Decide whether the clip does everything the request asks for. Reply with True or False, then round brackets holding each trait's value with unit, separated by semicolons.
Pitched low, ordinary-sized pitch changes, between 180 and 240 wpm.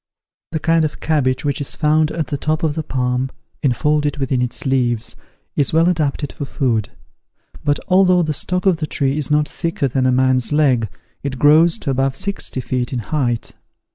False (145 Hz; 3.3 semitones; 190 wpm)